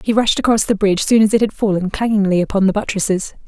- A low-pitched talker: No, high, 205 Hz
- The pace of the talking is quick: Yes, fast, 240 wpm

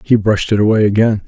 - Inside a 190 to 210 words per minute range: No, fast, 235 wpm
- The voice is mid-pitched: No, low, 105 Hz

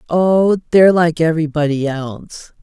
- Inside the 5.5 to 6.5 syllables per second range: No, 5.0 syllables/s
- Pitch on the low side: No, medium, 165 Hz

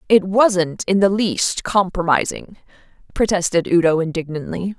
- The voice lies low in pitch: No, medium, 185 Hz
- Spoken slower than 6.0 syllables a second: Yes, 4.5 syllables/s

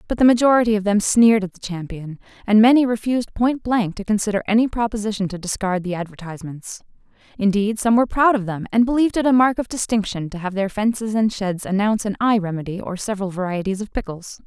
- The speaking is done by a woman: Yes, female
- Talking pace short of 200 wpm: No, fast, 205 wpm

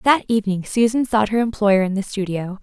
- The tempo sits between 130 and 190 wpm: No, fast, 205 wpm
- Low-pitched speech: No, high, 210 Hz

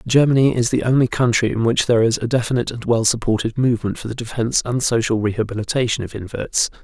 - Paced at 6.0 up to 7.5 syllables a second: Yes, 6.7 syllables/s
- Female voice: No, male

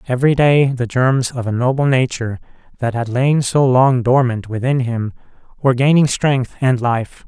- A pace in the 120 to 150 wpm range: No, average, 175 wpm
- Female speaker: No, male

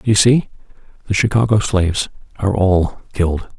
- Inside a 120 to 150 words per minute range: Yes, slow, 135 wpm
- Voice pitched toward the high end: No, low, 100 Hz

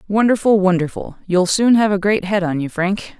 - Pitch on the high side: Yes, high, 195 Hz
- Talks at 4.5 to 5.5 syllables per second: Yes, 5.1 syllables/s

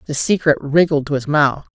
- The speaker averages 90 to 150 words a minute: No, fast, 205 wpm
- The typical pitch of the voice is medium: Yes, medium, 150 Hz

